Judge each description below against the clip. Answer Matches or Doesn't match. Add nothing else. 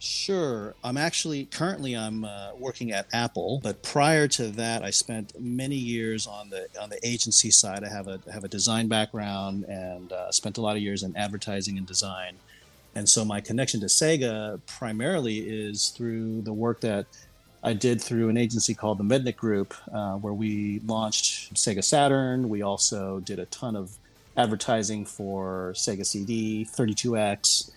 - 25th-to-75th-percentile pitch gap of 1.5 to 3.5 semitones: Matches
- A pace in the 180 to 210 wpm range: Doesn't match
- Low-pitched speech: Matches